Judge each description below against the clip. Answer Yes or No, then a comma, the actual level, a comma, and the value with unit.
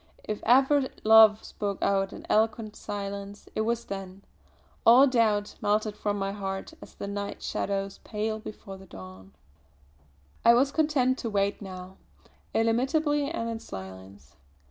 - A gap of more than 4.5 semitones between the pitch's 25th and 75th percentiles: No, average, 2.8 semitones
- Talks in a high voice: Yes, high, 210 Hz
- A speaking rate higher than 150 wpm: No, average, 145 wpm